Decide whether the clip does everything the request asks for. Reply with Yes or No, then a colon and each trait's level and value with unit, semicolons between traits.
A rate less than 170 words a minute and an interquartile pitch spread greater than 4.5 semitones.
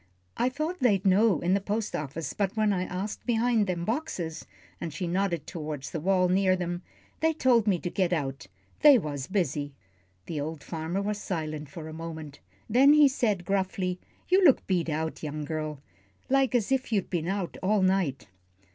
No: average, 185 wpm; average, 5.1 semitones